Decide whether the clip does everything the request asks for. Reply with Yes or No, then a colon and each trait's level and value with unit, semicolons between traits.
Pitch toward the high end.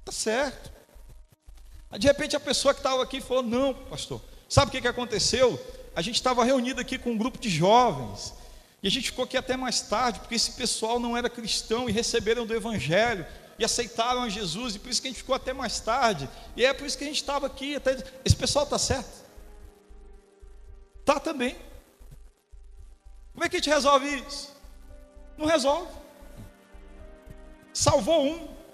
Yes: very high, 250 Hz